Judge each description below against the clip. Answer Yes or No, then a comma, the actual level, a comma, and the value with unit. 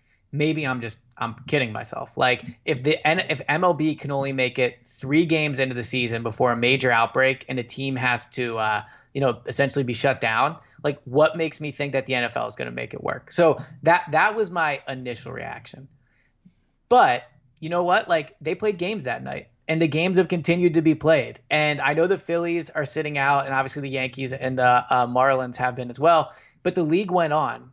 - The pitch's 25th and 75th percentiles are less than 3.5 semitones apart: No, average, 4.0 semitones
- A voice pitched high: No, low, 135 Hz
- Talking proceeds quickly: Yes, fast, 215 wpm